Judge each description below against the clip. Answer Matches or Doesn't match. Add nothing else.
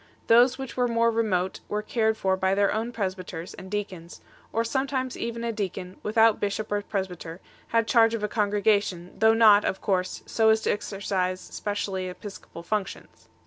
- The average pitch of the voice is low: Doesn't match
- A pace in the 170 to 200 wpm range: Matches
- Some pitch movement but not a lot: Matches